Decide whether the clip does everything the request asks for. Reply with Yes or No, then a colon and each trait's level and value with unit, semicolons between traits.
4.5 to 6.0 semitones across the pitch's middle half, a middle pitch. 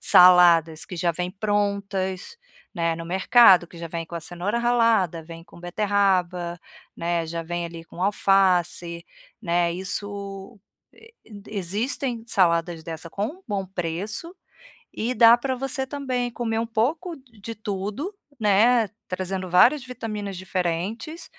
No: average, 4.9 semitones; high, 195 Hz